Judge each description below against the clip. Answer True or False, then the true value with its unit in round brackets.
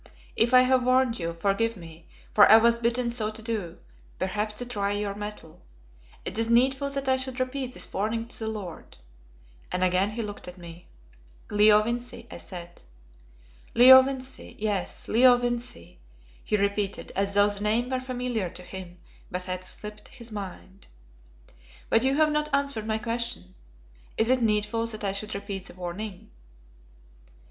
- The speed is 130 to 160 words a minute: False (170 wpm)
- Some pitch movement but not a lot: True (3.8 semitones)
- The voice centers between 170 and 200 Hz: False (215 Hz)